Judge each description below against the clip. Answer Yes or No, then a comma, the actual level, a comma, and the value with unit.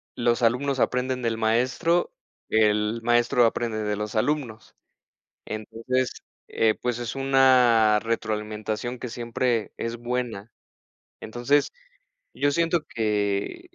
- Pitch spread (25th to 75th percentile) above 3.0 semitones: No, narrow, 2.5 semitones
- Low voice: Yes, low, 120 Hz